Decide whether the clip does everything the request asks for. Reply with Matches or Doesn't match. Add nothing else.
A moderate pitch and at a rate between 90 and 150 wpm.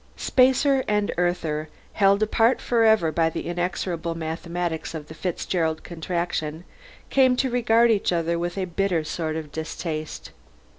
Matches